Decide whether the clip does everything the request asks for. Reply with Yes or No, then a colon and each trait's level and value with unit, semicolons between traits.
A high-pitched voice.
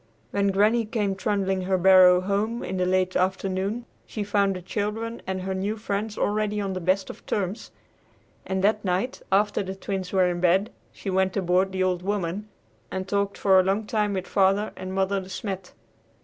Yes: high, 195 Hz